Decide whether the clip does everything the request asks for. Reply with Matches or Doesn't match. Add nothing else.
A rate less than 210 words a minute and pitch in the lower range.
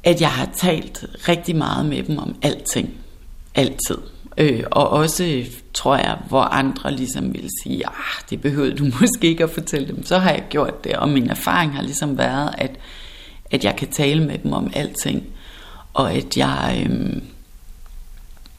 Doesn't match